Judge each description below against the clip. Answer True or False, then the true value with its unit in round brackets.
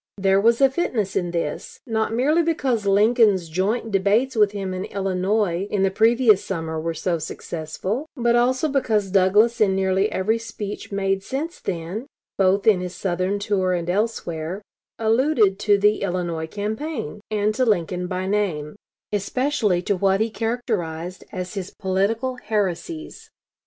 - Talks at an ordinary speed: True (150 wpm)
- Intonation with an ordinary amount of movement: True (3.5 semitones)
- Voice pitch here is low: False (200 Hz)